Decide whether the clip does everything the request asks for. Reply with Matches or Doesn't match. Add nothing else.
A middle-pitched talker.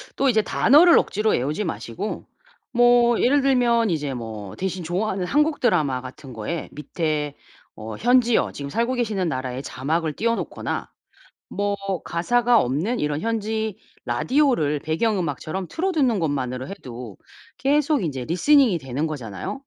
Matches